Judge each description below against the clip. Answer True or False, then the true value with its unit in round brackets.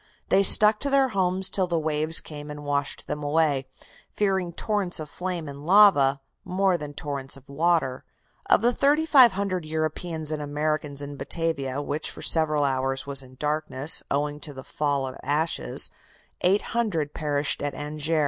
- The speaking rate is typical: True (160 wpm)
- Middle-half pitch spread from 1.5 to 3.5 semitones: False (4.0 semitones)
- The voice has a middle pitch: True (155 Hz)